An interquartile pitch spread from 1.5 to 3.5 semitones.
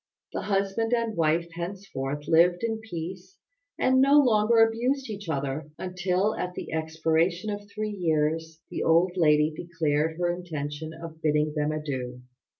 No: average, 4.7 semitones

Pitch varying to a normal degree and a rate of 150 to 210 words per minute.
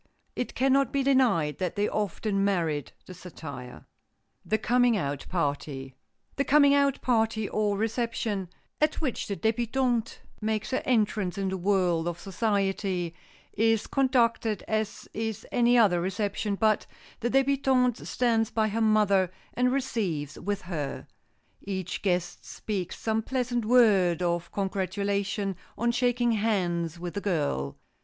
No: average, 4.6 semitones; average, 140 wpm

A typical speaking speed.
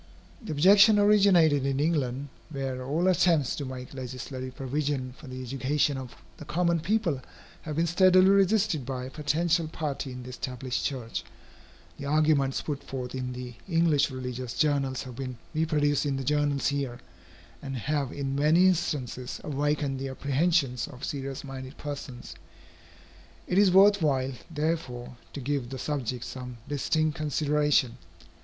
Yes: average, 150 wpm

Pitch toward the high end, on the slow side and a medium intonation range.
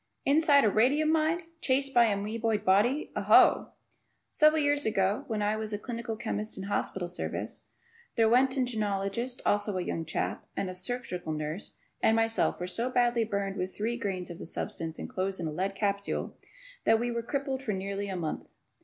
No: high, 215 Hz; average, 185 wpm; average, 4.1 semitones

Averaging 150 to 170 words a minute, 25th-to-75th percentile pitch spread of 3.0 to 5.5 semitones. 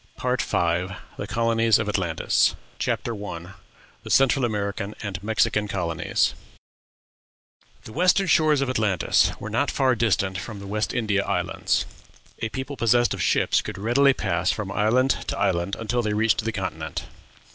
Yes: average, 155 wpm; average, 3.7 semitones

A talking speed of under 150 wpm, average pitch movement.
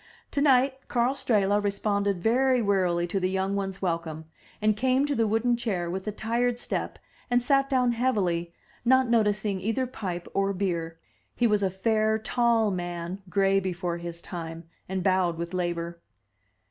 No: average, 160 wpm; average, 4.9 semitones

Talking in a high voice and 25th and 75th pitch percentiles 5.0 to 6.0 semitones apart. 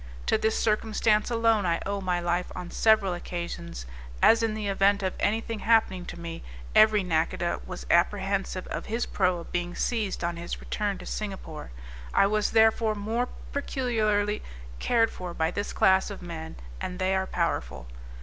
No: high, 195 Hz; average, 3.7 semitones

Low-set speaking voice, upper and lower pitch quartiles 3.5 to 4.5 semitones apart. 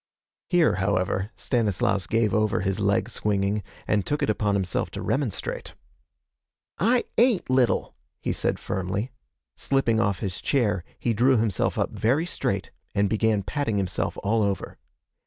Yes: low, 105 Hz; average, 3.8 semitones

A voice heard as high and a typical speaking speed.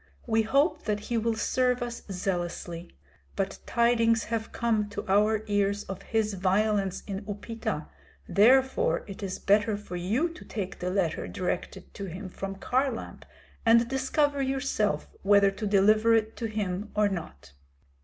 Yes: high, 210 Hz; average, 155 wpm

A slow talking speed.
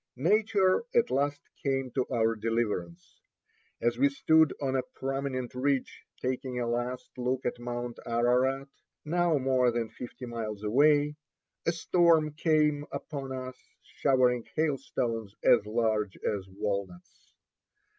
Yes: slow, 125 wpm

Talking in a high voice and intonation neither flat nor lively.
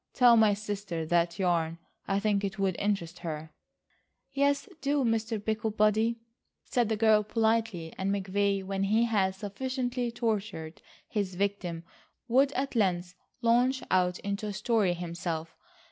Yes: high, 205 Hz; average, 3.7 semitones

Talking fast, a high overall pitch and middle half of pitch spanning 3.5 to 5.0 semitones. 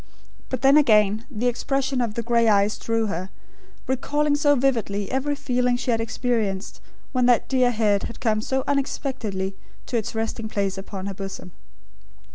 No: average, 165 wpm; high, 230 Hz; average, 4.0 semitones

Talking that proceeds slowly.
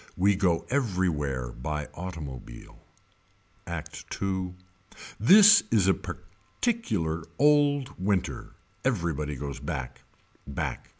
Yes: slow, 95 wpm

